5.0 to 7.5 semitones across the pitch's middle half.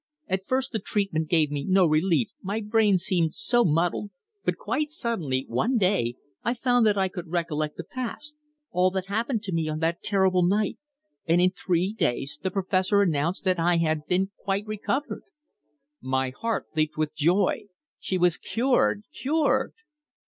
No: average, 4.6 semitones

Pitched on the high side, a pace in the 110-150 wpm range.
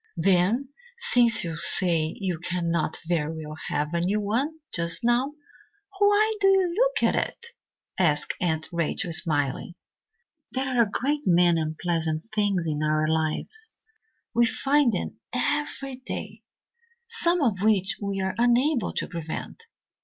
Yes: high, 195 Hz; average, 140 wpm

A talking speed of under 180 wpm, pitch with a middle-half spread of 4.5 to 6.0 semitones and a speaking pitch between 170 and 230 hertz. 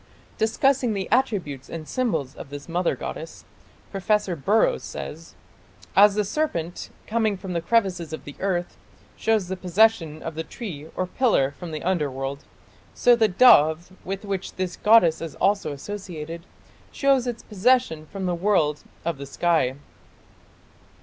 Yes: average, 150 wpm; average, 5.2 semitones; medium, 185 Hz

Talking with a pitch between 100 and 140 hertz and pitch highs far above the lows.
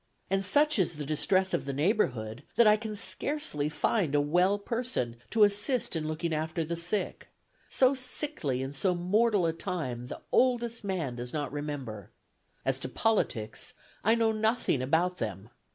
No: medium, 180 Hz; wide, 7.2 semitones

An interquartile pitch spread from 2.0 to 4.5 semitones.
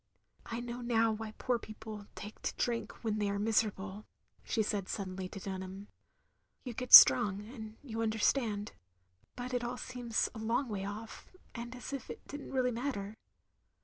Yes: average, 2.8 semitones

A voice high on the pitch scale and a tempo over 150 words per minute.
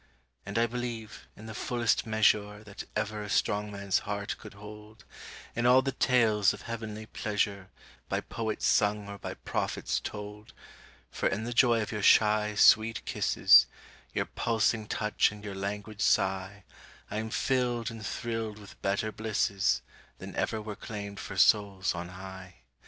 No: low, 105 Hz; average, 160 wpm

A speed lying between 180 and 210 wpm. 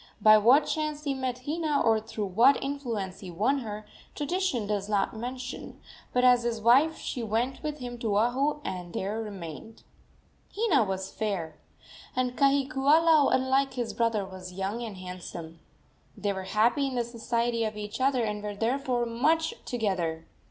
No: average, 165 wpm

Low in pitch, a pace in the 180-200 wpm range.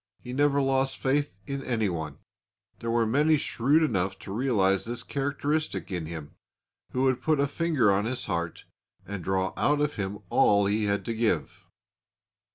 No: low, 120 Hz; average, 165 wpm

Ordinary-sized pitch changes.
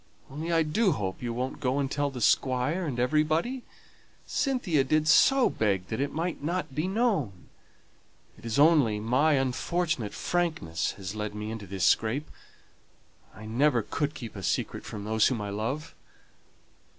No: wide, 6.5 semitones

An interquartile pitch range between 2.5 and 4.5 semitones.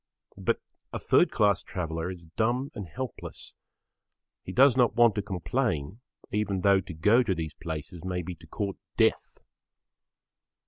No: average, 5.0 semitones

